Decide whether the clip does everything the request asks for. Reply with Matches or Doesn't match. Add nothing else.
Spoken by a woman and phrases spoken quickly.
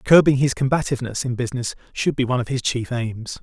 Doesn't match